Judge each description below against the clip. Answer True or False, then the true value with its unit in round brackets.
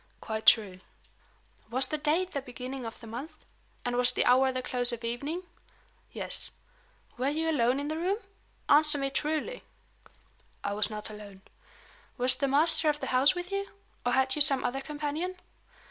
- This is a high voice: True (270 Hz)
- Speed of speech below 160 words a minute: False (175 wpm)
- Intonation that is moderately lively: True (3.9 semitones)